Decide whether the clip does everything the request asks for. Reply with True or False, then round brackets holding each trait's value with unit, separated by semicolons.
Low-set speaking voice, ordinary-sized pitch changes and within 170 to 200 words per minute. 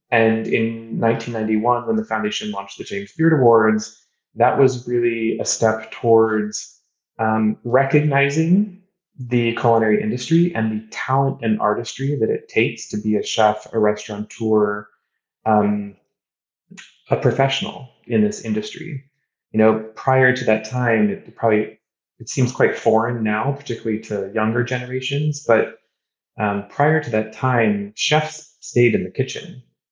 False (115 Hz; 3.8 semitones; 140 wpm)